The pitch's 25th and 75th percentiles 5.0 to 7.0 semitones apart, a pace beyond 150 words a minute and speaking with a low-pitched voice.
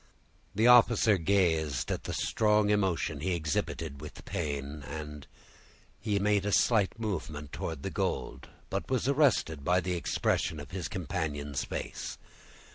No: wide, 5.4 semitones; average, 145 wpm; very low, 90 Hz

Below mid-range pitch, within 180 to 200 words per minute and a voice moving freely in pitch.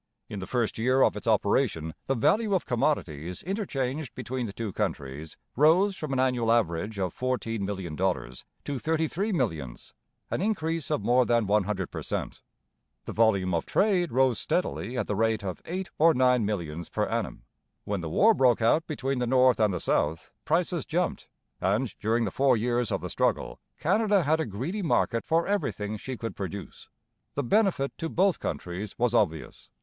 Yes: low, 120 Hz; average, 185 wpm; wide, 7.5 semitones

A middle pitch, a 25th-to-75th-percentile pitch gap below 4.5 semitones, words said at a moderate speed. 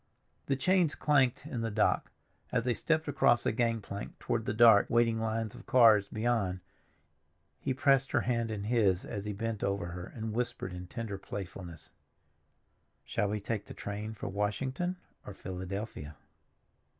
No: low, 110 Hz; average, 3.4 semitones; average, 160 wpm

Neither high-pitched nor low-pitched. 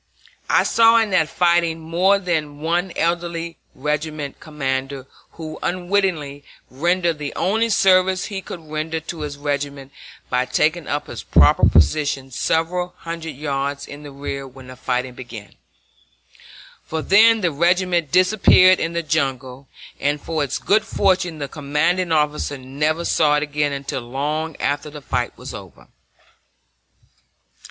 Yes: medium, 155 Hz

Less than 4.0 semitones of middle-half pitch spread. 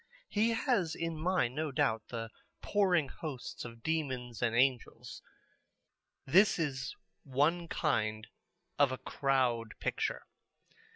No: wide, 5.4 semitones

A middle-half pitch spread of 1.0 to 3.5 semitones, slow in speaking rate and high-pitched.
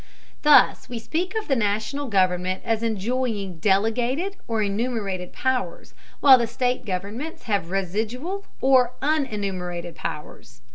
No: average, 5.1 semitones; slow, 125 wpm; high, 225 Hz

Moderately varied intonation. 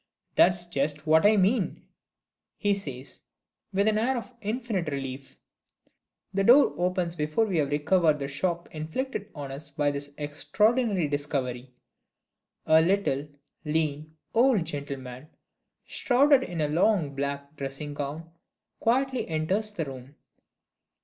No: wide, 6.0 semitones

